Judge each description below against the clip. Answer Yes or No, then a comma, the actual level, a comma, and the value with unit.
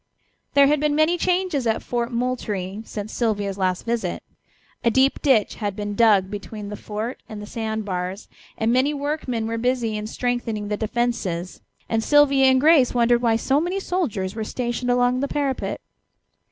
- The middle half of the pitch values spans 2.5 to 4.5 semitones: Yes, average, 4.1 semitones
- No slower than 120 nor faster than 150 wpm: No, average, 175 wpm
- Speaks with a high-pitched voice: Yes, high, 235 Hz